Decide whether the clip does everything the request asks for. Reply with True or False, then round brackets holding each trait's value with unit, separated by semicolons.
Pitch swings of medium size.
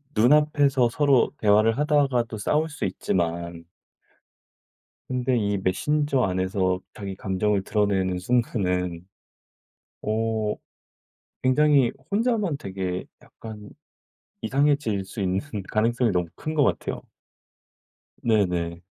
False (6.4 semitones)